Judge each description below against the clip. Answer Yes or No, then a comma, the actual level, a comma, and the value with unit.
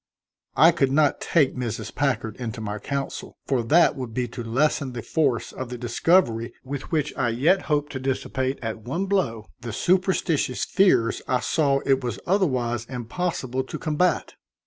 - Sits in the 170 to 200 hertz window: No, low, 130 Hz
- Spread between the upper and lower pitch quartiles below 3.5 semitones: No, average, 4.3 semitones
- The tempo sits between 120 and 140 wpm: No, average, 170 wpm